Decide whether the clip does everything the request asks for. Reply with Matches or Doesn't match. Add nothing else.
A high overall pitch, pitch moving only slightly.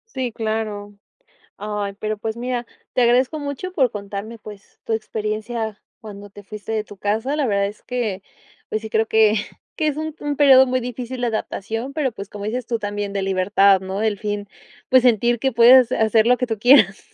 Doesn't match